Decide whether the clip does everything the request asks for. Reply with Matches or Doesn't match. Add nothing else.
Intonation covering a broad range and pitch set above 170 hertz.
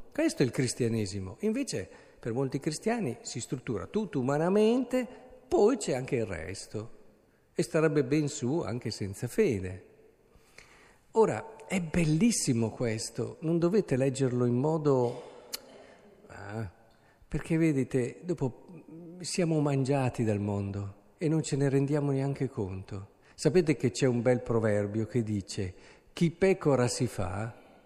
Doesn't match